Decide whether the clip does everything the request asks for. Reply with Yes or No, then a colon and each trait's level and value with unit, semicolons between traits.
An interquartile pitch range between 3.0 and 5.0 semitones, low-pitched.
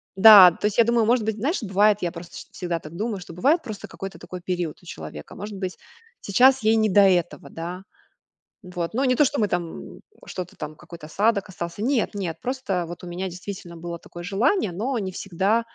No: average, 4.1 semitones; high, 195 Hz